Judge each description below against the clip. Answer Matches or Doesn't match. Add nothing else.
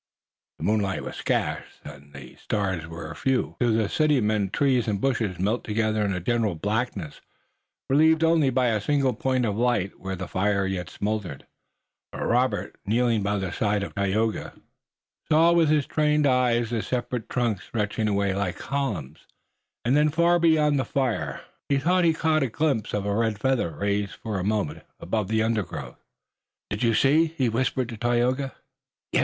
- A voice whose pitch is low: Matches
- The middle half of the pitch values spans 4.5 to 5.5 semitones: Matches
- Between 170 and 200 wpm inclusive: Matches